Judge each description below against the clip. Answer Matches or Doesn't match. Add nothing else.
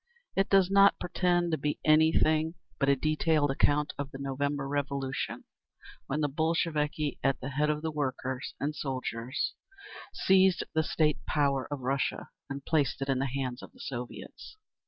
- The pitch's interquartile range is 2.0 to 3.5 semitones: Matches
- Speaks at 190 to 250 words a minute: Doesn't match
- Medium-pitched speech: Matches